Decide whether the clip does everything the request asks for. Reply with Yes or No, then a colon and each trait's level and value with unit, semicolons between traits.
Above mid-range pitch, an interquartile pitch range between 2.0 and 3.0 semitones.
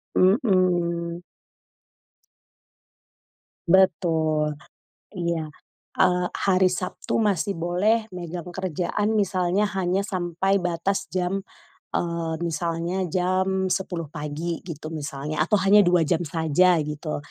No: medium, 175 Hz; narrow, 2.4 semitones